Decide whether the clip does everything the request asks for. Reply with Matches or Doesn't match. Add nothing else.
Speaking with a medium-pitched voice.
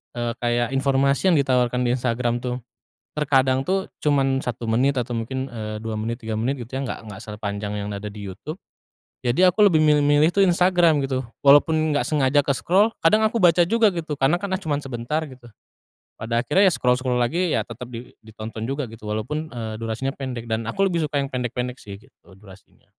Doesn't match